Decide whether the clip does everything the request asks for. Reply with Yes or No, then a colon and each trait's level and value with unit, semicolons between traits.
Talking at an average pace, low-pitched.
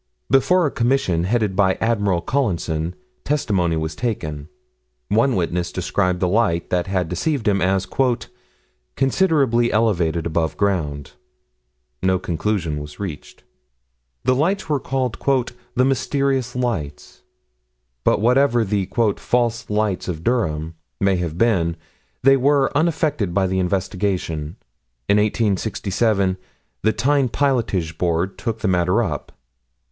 No: slow, 120 wpm; low, 100 Hz